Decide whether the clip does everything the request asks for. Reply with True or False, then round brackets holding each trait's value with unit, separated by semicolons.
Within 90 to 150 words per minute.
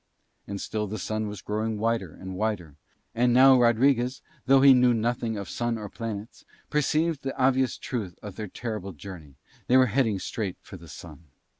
False (180 wpm)